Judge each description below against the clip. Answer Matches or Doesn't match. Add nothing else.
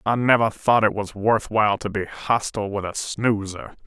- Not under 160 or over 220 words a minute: Matches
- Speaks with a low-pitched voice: Matches